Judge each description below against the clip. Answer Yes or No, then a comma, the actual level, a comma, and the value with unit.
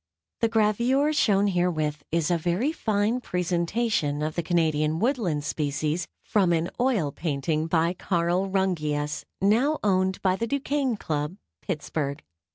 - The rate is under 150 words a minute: Yes, slow, 135 wpm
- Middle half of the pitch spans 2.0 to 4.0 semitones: No, wide, 5.5 semitones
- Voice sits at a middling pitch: Yes, medium, 180 Hz